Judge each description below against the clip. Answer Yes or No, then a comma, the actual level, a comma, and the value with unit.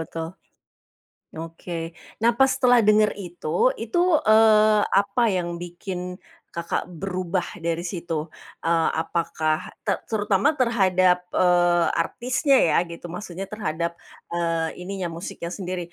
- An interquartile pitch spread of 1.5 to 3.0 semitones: No, average, 3.8 semitones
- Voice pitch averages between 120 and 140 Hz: No, medium, 185 Hz